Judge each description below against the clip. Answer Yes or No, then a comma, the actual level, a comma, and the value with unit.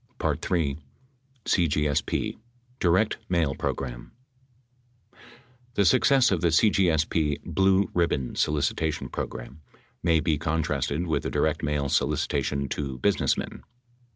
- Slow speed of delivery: Yes, slow, 100 wpm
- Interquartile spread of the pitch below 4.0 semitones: Yes, average, 3.5 semitones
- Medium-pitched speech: No, very low, 80 Hz